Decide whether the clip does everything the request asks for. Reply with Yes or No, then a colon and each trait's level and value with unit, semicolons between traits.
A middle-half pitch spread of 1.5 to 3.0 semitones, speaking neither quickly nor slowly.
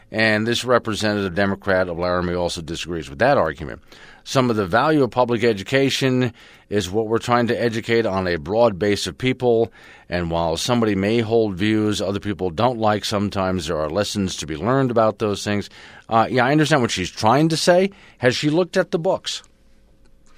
No: average, 4.0 semitones; average, 190 wpm